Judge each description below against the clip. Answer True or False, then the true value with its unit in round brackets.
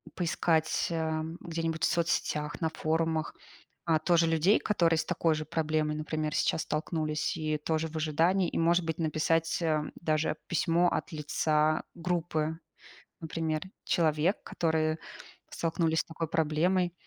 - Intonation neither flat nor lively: False (1.3 semitones)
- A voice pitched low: False (160 Hz)